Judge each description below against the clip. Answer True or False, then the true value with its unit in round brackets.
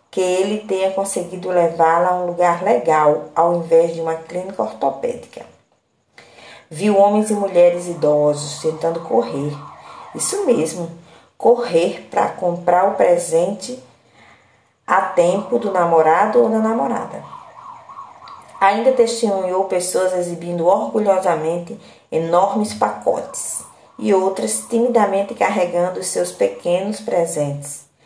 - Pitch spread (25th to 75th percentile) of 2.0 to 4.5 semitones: True (3.6 semitones)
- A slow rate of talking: True (110 wpm)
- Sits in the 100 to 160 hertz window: False (180 Hz)